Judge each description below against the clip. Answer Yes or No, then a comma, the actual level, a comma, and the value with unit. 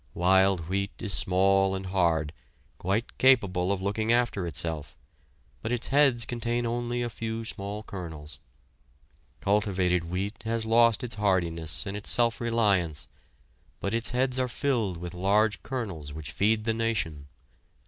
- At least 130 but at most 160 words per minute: Yes, average, 145 wpm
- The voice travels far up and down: No, average, 4.4 semitones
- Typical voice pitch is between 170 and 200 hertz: No, low, 100 Hz